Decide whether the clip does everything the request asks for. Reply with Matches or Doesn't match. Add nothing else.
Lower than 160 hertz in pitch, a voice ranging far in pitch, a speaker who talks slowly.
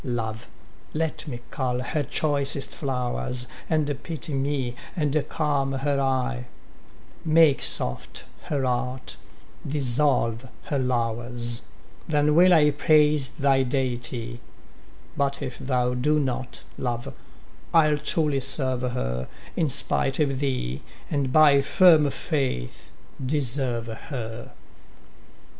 Doesn't match